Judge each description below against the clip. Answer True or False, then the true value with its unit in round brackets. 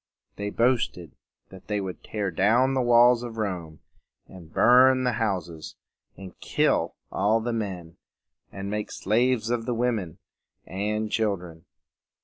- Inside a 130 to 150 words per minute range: True (135 wpm)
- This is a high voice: False (105 Hz)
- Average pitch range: True (4.2 semitones)